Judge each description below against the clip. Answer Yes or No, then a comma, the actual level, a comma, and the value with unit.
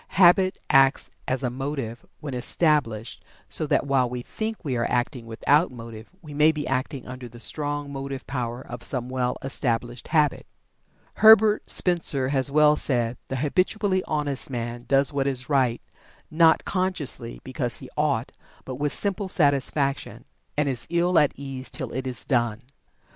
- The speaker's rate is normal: Yes, average, 160 wpm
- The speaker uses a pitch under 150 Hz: Yes, low, 135 Hz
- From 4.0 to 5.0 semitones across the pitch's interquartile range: No, average, 3.6 semitones